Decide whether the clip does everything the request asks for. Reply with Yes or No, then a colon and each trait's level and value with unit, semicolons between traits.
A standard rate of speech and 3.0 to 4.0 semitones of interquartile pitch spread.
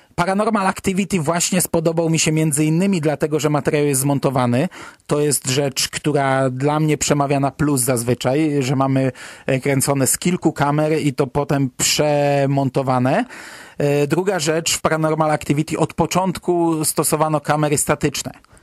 No: average, 140 wpm; narrow, 2.5 semitones